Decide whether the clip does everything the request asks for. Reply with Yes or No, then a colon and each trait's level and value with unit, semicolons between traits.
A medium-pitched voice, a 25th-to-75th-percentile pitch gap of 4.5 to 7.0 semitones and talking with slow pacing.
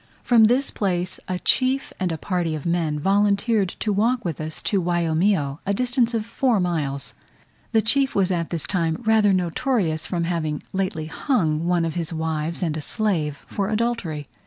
No: medium, 180 Hz; average, 5.1 semitones; average, 180 wpm